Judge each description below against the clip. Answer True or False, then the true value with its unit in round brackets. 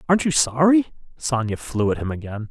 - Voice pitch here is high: False (135 Hz)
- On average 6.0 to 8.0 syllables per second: False (5.7 syllables/s)